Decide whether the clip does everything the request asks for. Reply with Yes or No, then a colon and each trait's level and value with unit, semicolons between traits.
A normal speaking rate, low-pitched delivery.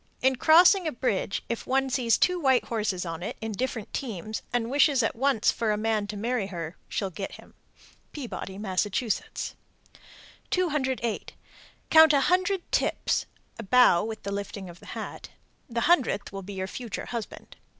No: average, 170 wpm; high, 230 Hz